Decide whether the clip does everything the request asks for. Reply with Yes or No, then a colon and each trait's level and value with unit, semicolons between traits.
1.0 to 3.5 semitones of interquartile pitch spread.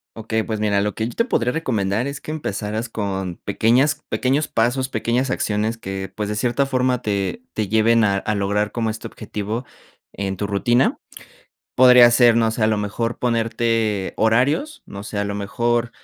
Yes: average, 2.9 semitones